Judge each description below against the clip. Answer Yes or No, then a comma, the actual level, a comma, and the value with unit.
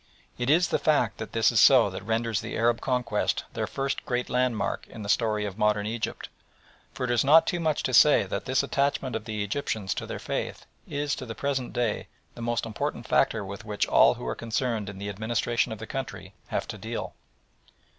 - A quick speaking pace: Yes, fast, 215 wpm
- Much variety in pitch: No, average, 3.6 semitones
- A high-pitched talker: No, low, 115 Hz